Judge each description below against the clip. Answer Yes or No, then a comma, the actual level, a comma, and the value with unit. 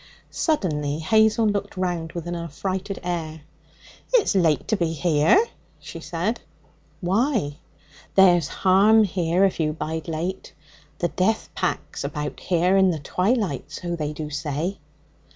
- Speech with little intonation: No, average, 3.7 semitones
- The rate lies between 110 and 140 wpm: Yes, slow, 135 wpm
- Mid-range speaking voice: Yes, medium, 175 Hz